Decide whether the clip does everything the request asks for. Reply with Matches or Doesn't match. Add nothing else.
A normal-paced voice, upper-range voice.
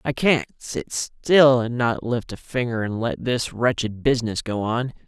Doesn't match